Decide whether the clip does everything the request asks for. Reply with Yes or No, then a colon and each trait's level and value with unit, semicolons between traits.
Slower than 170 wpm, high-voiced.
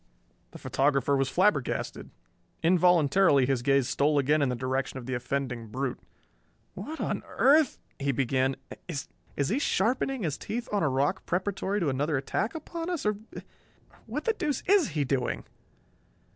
No: average, 160 wpm; medium, 145 Hz